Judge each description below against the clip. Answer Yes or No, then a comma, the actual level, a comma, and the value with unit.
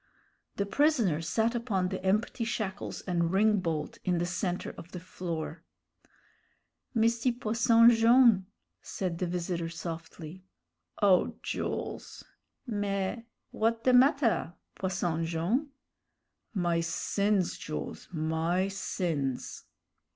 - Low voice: No, high, 190 Hz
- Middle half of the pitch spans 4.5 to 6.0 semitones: Yes, average, 5.0 semitones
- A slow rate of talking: Yes, slow, 105 wpm